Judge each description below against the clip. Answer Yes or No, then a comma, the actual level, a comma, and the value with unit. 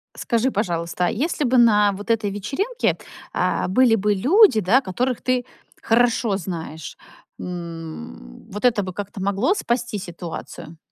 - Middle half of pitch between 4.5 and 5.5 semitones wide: Yes, average, 5.2 semitones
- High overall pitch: Yes, high, 205 Hz